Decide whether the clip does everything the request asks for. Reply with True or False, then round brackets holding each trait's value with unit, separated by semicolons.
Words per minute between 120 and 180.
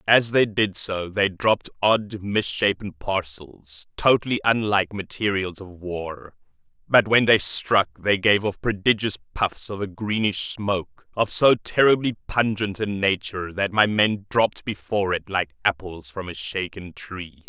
True (155 wpm)